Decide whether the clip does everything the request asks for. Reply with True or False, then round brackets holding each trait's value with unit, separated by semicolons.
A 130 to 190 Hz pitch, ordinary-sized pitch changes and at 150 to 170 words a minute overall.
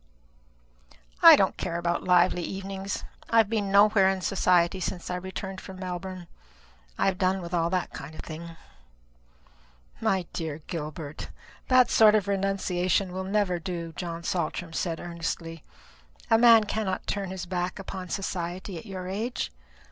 False (185 Hz; 2.2 semitones; 155 wpm)